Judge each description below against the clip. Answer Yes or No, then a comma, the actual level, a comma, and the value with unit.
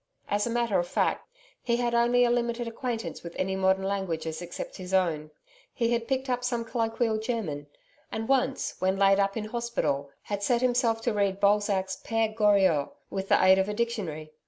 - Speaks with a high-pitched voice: Yes, high, 210 Hz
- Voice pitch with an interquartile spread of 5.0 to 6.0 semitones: No, average, 3.8 semitones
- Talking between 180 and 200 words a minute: Yes, average, 190 wpm